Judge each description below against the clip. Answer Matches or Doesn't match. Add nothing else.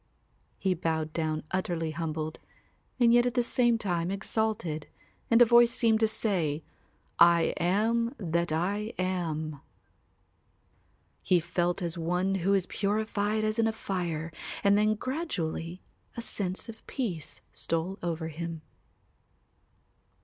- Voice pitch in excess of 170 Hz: Matches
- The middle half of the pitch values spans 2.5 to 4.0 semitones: Doesn't match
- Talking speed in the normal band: Doesn't match